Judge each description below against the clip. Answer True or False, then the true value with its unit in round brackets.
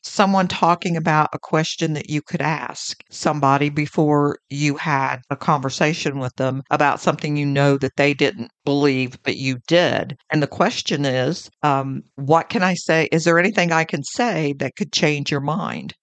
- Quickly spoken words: False (180 wpm)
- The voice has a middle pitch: True (150 Hz)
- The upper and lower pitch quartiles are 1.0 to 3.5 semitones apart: True (2.8 semitones)